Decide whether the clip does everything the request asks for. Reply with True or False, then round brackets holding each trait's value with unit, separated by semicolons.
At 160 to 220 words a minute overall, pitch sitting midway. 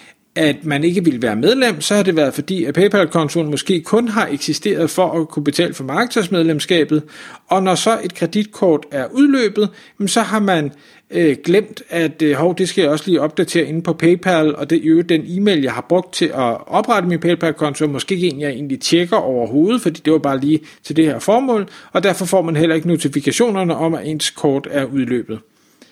True (205 wpm; 165 Hz)